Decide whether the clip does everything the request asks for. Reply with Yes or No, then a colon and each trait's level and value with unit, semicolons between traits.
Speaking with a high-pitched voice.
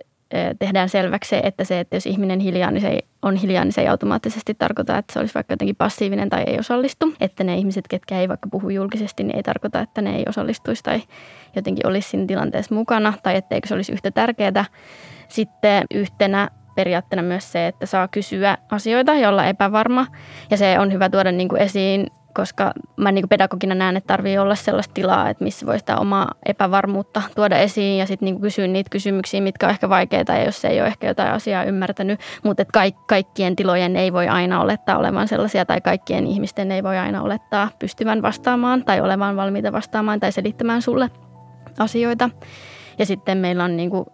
Yes: high, 195 Hz